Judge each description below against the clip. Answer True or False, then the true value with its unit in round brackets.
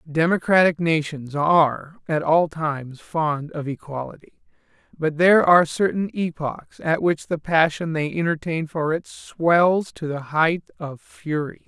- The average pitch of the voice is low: False (160 Hz)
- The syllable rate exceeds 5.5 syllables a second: False (4.2 syllables/s)